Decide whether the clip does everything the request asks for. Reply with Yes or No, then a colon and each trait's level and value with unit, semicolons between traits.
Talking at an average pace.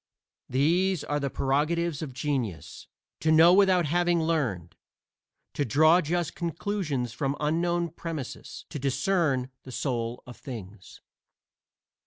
No: slow, 120 wpm